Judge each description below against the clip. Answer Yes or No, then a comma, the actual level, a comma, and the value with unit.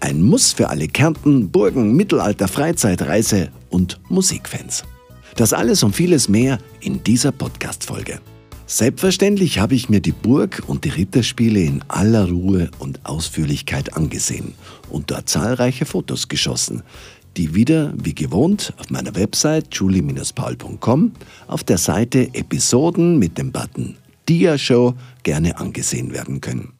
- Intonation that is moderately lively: No, wide, 8.1 semitones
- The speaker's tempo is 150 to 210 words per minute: No, average, 135 wpm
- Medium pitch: No, low, 115 Hz